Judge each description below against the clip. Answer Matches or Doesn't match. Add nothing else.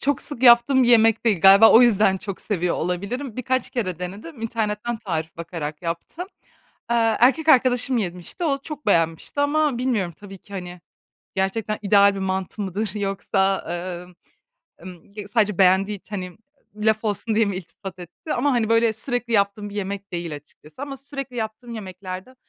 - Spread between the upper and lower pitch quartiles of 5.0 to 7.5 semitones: Doesn't match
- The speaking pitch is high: Matches